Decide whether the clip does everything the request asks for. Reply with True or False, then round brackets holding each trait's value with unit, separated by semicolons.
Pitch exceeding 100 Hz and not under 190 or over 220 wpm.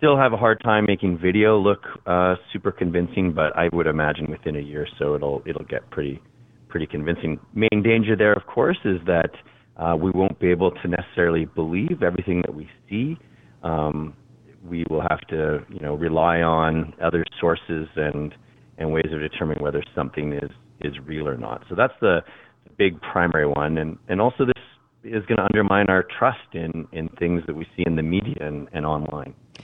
False (85 Hz; 195 wpm)